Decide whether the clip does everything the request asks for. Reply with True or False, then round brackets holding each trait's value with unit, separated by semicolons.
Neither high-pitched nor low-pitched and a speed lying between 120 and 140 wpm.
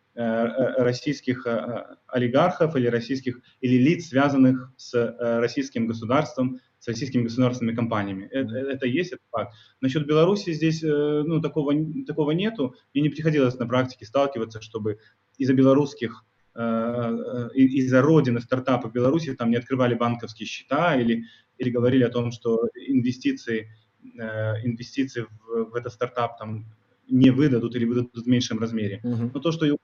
False (125 Hz; 135 wpm)